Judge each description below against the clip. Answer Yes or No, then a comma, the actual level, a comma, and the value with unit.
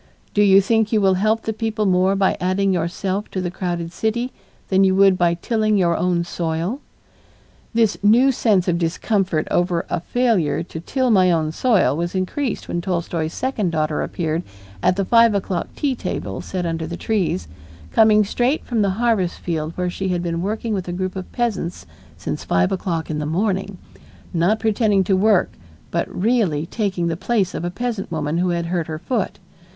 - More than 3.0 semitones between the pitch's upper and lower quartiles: Yes, average, 4.0 semitones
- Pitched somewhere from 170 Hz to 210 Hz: Yes, medium, 185 Hz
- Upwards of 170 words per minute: Yes, average, 190 wpm